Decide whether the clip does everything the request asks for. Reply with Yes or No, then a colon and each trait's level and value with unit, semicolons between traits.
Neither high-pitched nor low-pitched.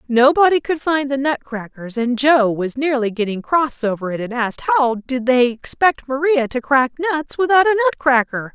No: very high, 270 Hz